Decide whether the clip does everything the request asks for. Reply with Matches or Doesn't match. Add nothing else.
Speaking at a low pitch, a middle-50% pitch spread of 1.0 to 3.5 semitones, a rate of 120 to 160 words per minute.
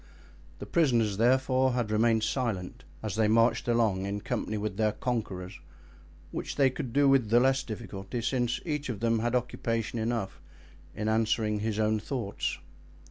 Matches